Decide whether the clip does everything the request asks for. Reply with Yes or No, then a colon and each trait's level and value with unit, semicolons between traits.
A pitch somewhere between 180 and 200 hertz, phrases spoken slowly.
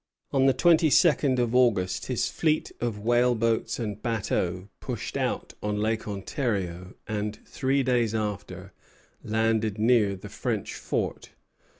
No: low, 110 Hz; slow, 130 wpm